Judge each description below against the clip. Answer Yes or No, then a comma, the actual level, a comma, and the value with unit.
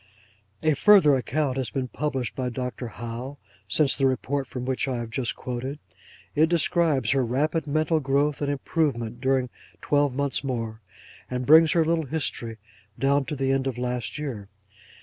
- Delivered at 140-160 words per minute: No, average, 170 wpm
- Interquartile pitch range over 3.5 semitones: No, average, 3.0 semitones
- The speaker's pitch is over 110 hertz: Yes, low, 135 Hz